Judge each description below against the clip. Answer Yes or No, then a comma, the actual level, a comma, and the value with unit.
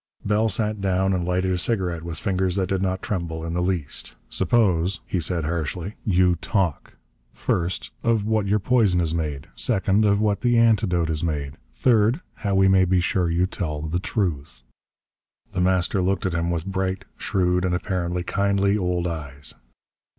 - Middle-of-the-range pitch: No, very low, 90 Hz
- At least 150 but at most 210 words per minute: Yes, average, 175 wpm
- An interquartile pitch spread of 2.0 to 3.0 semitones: Yes, average, 2.7 semitones